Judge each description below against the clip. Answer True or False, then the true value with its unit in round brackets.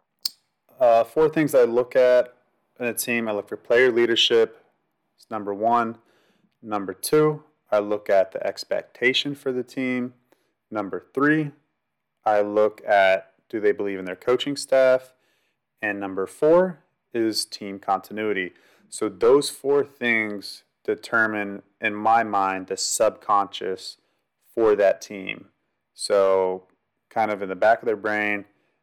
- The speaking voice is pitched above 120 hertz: False (115 Hz)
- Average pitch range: True (4.9 semitones)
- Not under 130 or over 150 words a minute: True (140 wpm)